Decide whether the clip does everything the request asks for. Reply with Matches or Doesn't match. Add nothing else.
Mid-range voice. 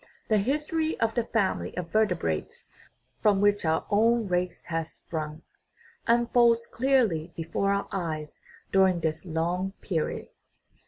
Doesn't match